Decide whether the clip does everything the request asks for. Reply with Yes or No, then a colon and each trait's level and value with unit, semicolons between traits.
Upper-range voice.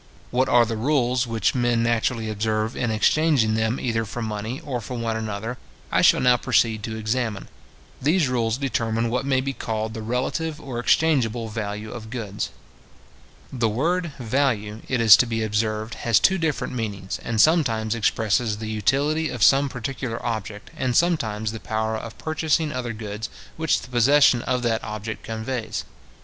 No: low, 115 Hz